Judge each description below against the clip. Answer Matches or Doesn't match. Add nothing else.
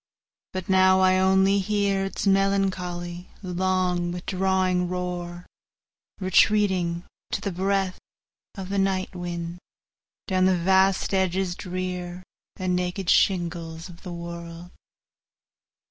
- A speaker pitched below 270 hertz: Matches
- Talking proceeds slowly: Matches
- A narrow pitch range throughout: Matches